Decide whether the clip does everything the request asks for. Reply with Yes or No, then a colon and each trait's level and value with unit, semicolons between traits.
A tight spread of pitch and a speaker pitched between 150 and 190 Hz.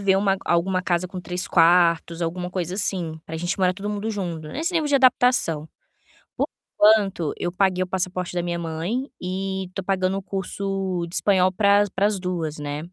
Yes: narrow, 2.2 semitones; medium, 185 Hz